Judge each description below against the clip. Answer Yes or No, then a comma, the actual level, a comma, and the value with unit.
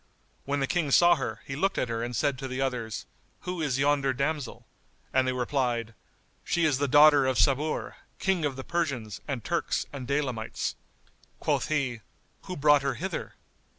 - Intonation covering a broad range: No, average, 2.9 semitones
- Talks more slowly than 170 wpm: No, average, 180 wpm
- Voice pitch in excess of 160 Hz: No, medium, 140 Hz